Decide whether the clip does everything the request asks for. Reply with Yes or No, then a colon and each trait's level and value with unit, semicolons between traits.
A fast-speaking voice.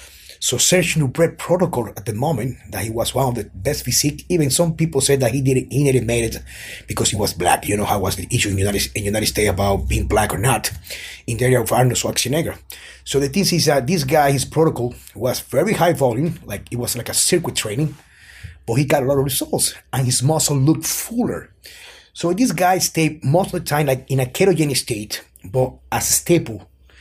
Yes: fast, 225 wpm